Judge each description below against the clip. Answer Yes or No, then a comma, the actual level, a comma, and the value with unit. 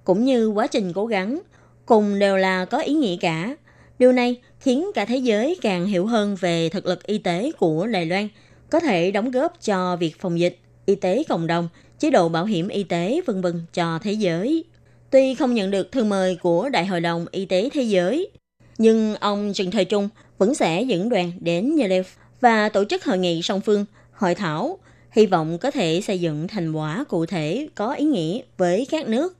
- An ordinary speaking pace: Yes, average, 210 wpm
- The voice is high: Yes, high, 195 Hz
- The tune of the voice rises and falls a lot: Yes, wide, 5.8 semitones